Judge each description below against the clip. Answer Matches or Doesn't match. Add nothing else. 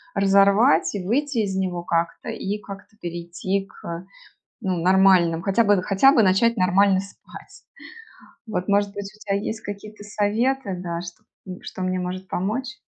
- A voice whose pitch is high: Matches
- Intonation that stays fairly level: Matches